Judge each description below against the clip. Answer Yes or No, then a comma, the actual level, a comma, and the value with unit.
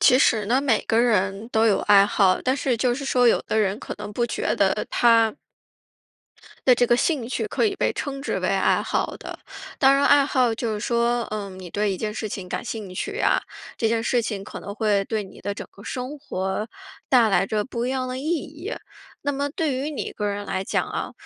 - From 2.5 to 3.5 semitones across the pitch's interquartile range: No, average, 4.1 semitones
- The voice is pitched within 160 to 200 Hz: No, high, 230 Hz